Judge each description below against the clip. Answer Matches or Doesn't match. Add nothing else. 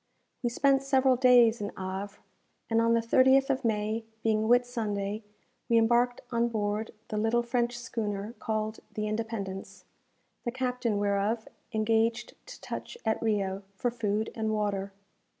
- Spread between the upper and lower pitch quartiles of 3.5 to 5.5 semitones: Doesn't match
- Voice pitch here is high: Matches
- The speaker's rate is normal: Matches